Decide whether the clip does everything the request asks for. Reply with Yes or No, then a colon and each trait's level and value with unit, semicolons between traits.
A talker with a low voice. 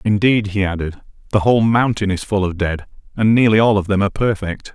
Yes: low, 105 Hz